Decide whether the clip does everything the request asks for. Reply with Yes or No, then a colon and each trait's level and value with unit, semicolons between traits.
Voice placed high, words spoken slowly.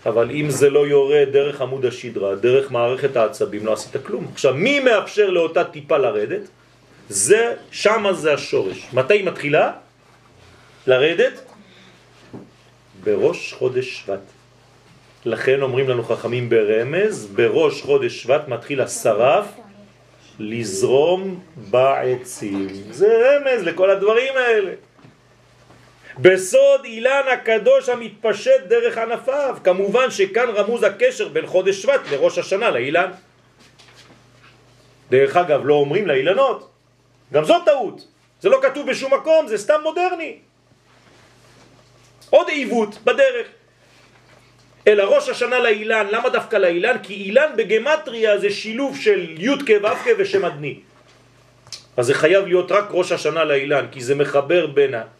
Yes: high, 230 Hz; slow, 120 wpm